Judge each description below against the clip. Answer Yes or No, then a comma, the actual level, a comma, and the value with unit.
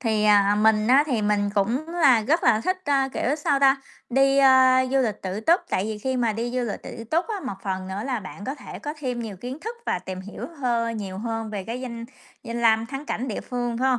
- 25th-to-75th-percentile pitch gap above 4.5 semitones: No, average, 4.0 semitones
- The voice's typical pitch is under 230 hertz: No, high, 235 Hz